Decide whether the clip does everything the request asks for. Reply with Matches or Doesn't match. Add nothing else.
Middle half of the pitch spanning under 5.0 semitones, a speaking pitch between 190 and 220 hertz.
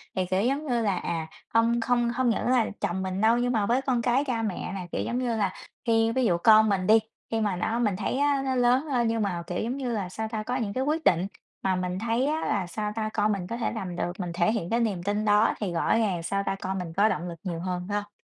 Matches